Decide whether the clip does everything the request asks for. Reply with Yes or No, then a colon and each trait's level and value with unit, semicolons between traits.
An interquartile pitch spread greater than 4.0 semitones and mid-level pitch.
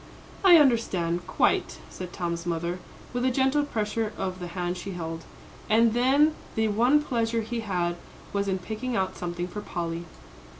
No: average, 5.2 semitones; high, 205 Hz